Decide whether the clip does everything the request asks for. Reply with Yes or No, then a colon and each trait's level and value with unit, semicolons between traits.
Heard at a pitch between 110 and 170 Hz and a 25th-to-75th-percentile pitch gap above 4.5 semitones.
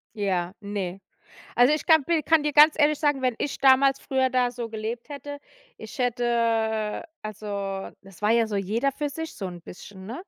No: high, 240 Hz; average, 5.3 semitones